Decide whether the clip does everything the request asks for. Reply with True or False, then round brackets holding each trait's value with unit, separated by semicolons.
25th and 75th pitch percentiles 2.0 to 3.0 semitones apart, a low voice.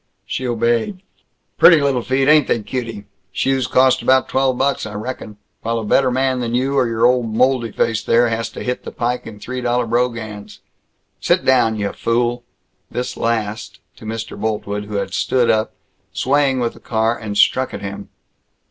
True (2.7 semitones; 120 Hz)